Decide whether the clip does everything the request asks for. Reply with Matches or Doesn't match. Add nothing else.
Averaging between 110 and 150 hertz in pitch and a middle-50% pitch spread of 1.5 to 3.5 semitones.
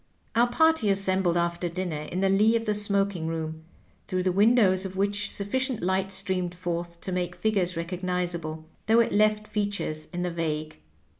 Doesn't match